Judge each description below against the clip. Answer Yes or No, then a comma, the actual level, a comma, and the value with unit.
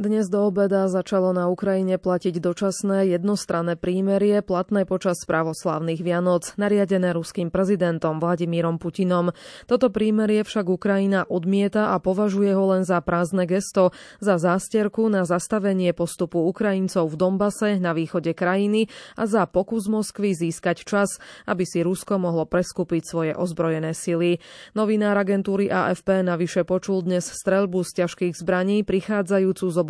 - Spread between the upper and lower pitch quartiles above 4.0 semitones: No, narrow, 2.4 semitones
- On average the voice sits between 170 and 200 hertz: Yes, medium, 185 Hz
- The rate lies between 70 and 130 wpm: No, average, 140 wpm